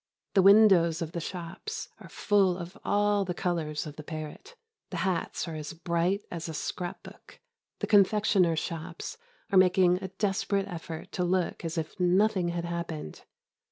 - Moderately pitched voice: Yes, medium, 175 Hz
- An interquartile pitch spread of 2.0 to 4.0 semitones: Yes, average, 2.7 semitones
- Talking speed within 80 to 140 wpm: No, average, 165 wpm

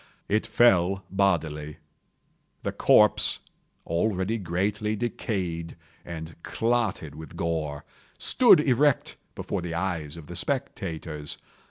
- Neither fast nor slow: No, slow, 105 wpm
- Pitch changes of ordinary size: Yes, average, 4.8 semitones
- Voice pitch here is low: Yes, very low, 90 Hz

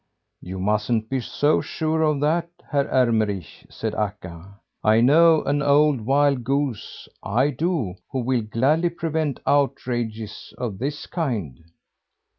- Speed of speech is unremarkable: No, slow, 130 wpm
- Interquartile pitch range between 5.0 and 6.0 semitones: Yes, wide, 5.4 semitones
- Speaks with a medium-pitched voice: No, low, 130 Hz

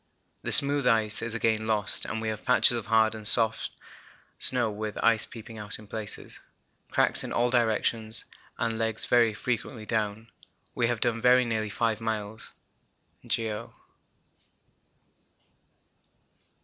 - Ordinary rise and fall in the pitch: No, narrow, 1.4 semitones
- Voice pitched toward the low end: Yes, low, 110 Hz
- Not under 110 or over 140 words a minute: Yes, slow, 135 wpm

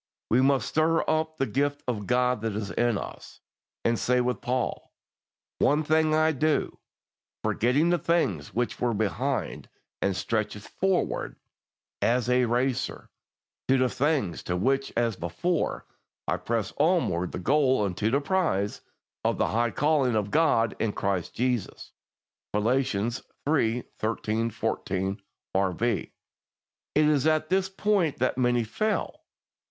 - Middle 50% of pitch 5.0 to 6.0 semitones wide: Yes, wide, 5.6 semitones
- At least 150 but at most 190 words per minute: No, average, 140 wpm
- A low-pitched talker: Yes, low, 125 Hz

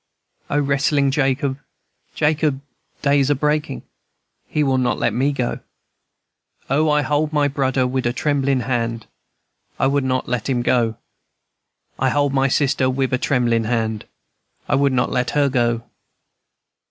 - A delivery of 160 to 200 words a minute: No, average, 150 wpm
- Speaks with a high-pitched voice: No, low, 135 Hz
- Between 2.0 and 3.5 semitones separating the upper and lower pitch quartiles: Yes, narrow, 2.4 semitones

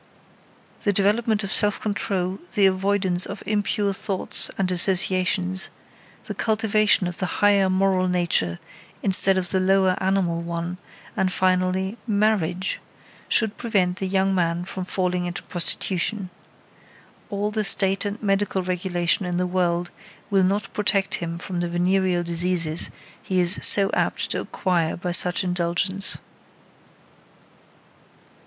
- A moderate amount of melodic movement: No, narrow, 1.9 semitones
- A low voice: No, medium, 185 Hz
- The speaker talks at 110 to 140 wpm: Yes, slow, 135 wpm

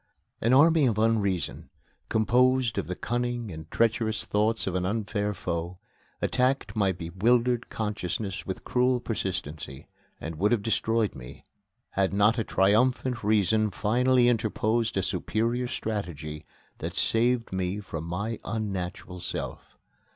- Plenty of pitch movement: No, average, 3.9 semitones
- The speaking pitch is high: No, low, 110 Hz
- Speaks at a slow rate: Yes, slow, 130 wpm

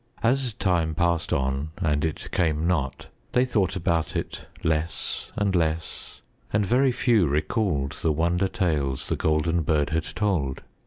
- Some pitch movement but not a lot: Yes, average, 4.2 semitones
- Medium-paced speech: Yes, average, 150 wpm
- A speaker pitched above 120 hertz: No, very low, 85 Hz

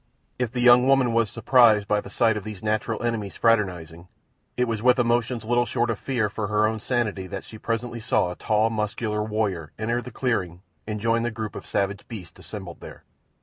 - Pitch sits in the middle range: No, low, 110 Hz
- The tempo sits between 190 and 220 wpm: Yes, fast, 205 wpm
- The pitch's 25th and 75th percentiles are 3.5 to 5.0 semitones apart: No, narrow, 2.4 semitones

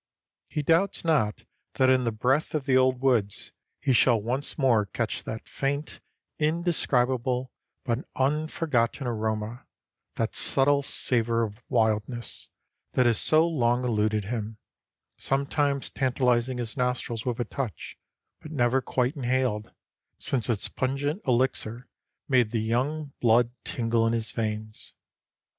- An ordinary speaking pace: No, slow, 130 wpm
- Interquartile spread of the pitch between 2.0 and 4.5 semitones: Yes, average, 3.1 semitones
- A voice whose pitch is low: Yes, low, 125 Hz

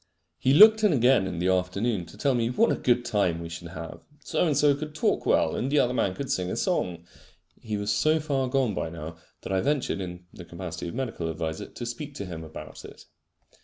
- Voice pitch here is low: Yes, low, 105 Hz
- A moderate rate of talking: No, fast, 235 wpm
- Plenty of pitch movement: Yes, wide, 7.9 semitones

